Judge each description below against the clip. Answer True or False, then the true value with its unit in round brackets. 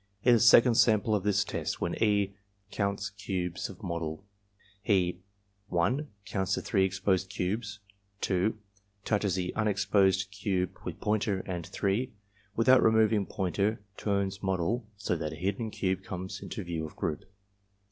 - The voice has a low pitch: True (100 Hz)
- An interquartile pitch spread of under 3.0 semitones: True (2.5 semitones)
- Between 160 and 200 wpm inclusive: False (145 wpm)